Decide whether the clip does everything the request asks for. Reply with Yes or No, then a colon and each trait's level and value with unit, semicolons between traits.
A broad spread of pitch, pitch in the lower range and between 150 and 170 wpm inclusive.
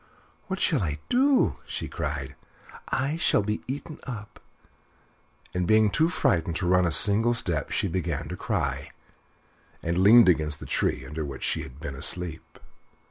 Yes: wide, 6.9 semitones; very low, 95 Hz; average, 160 wpm